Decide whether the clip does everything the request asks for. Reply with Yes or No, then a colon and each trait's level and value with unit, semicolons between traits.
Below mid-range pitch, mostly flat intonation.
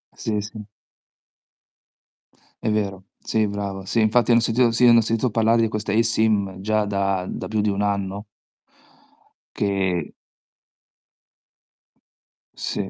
Yes: low, 105 Hz; narrow, 2.2 semitones